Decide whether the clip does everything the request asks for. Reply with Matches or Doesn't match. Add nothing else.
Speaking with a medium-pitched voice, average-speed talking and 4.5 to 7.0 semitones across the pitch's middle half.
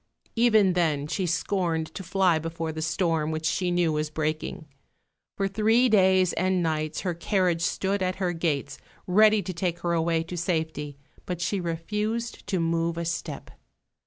Doesn't match